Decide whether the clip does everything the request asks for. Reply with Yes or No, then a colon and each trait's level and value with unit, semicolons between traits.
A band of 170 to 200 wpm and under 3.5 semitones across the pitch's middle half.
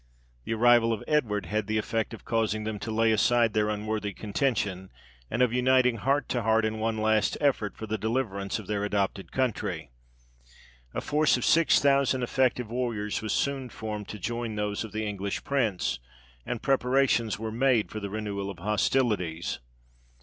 Yes: average, 175 wpm; average, 2.9 semitones